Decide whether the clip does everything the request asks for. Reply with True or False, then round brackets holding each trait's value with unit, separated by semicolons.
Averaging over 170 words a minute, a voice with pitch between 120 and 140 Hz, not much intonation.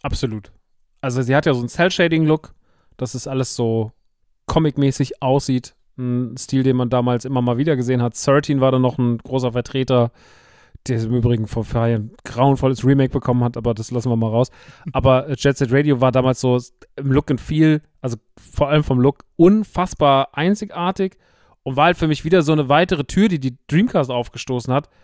False (190 wpm; 130 Hz; 3.1 semitones)